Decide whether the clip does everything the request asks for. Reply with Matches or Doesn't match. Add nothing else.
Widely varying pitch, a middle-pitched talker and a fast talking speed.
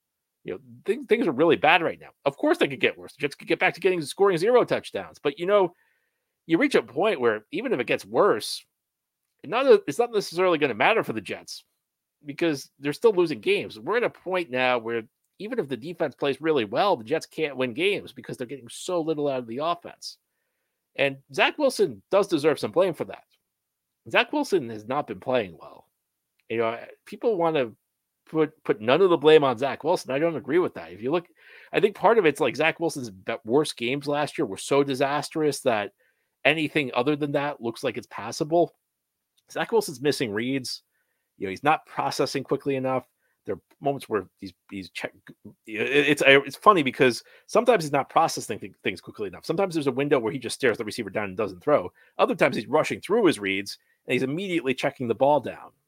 Matches